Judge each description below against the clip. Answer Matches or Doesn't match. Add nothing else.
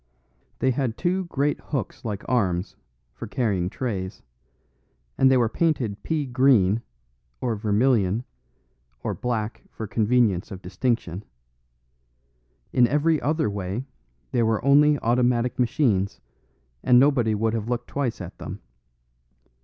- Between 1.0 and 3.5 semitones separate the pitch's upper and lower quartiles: Doesn't match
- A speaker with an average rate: Doesn't match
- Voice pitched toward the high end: Doesn't match